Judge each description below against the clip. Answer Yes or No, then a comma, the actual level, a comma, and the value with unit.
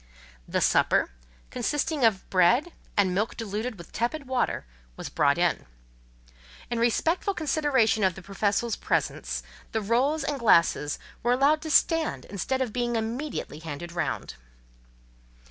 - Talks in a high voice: Yes, high, 235 Hz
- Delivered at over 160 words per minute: No, slow, 135 wpm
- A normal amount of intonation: No, wide, 5.8 semitones